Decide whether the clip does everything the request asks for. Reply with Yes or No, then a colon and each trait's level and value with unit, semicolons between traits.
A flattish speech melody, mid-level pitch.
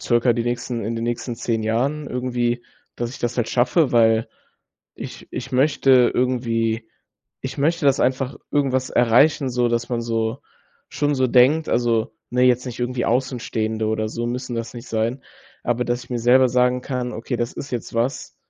No: narrow, 1.7 semitones; low, 120 Hz